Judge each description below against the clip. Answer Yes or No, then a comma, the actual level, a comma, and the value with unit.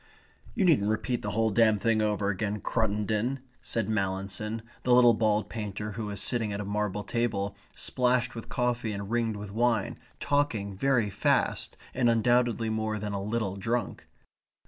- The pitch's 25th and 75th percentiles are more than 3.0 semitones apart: No, narrow, 2.5 semitones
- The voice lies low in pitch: Yes, low, 110 Hz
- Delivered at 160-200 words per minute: Yes, average, 165 wpm